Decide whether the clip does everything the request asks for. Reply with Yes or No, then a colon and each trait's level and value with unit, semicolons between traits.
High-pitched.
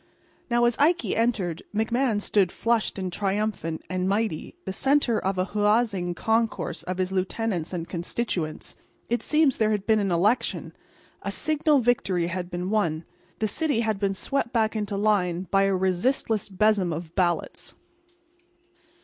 Yes: high, 205 Hz